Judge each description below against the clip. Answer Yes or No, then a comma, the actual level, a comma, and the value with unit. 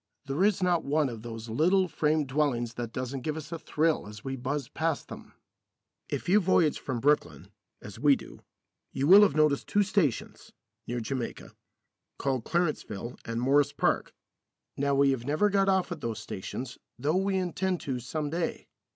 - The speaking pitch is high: No, medium, 145 Hz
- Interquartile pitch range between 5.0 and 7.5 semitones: Yes, wide, 5.5 semitones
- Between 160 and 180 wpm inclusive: Yes, average, 175 wpm